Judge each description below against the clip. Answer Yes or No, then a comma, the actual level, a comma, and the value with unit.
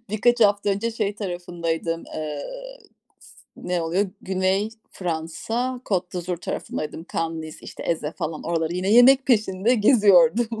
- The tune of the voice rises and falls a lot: No, average, 4.5 semitones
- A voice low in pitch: No, medium, 185 Hz